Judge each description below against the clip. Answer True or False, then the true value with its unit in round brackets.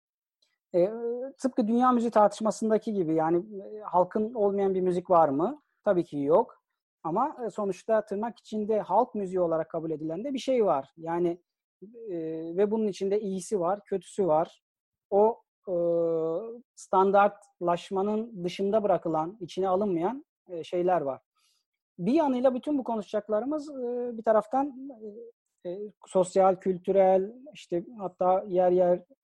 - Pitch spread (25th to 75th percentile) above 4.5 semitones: False (4.0 semitones)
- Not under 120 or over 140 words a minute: True (135 wpm)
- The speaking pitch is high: True (200 Hz)